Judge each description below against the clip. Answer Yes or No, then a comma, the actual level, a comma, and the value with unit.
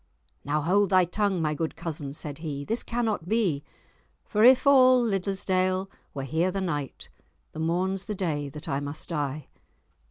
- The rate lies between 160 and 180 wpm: Yes, average, 165 wpm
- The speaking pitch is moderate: Yes, medium, 175 Hz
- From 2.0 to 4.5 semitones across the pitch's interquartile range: No, average, 4.9 semitones